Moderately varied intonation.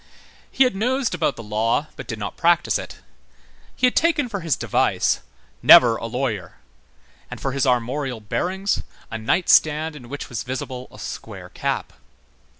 No: wide, 7.7 semitones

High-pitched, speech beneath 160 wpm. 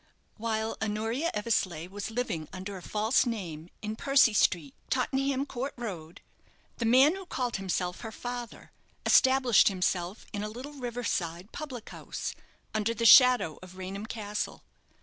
Yes: high, 220 Hz; average, 150 wpm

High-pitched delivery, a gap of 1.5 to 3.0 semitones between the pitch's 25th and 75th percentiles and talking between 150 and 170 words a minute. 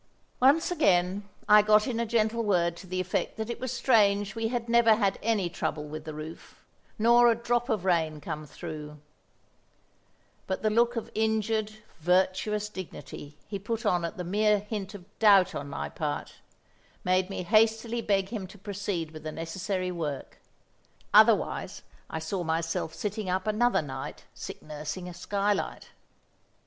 No: high, 200 Hz; average, 4.2 semitones; average, 160 wpm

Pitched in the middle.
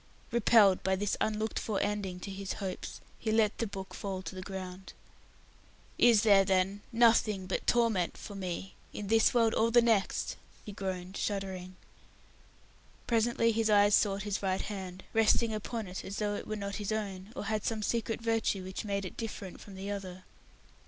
No: high, 205 Hz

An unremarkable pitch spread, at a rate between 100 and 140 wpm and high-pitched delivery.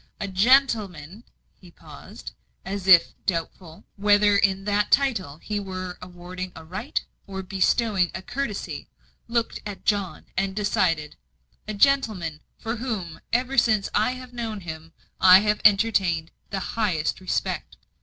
Yes: average, 3.3 semitones; slow, 135 wpm; high, 195 Hz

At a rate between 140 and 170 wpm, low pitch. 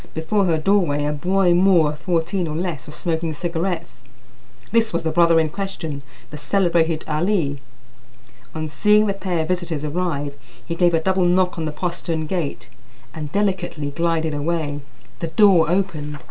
No: average, 165 wpm; medium, 165 Hz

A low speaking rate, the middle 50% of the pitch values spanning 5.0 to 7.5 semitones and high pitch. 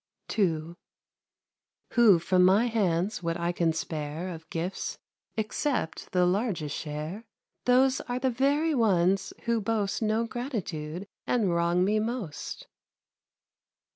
Yes: slow, 120 wpm; average, 5.3 semitones; high, 195 Hz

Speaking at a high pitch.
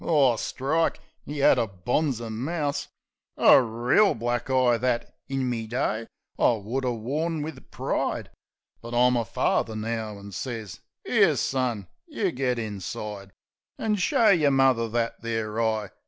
No: low, 120 Hz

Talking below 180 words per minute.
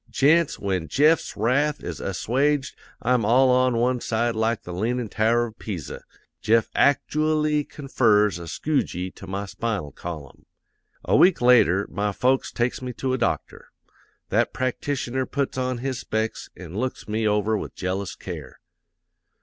Yes: average, 155 wpm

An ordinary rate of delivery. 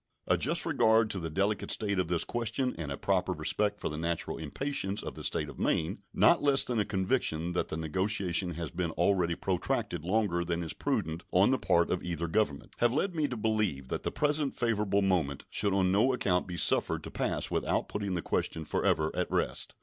No: fast, 210 wpm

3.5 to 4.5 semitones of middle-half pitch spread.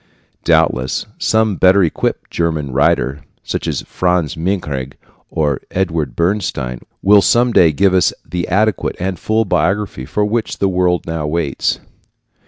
No: average, 4.9 semitones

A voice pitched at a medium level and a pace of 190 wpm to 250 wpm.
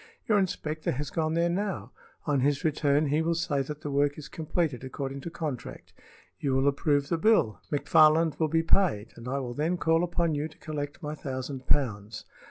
Yes: medium, 150 Hz; average, 195 wpm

